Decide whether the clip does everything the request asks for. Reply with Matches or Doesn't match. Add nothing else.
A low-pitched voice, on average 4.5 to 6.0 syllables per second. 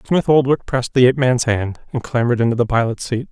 Doesn't match